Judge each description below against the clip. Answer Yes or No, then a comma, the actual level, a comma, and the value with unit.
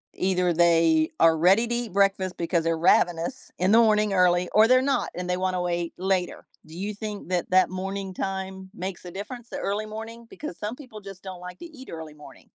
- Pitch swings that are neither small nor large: Yes, average, 3.2 semitones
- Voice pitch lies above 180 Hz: Yes, high, 190 Hz